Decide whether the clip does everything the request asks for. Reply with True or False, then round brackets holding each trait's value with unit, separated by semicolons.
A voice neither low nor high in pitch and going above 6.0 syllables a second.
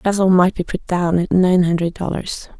False (180 Hz; 4.9 syllables/s)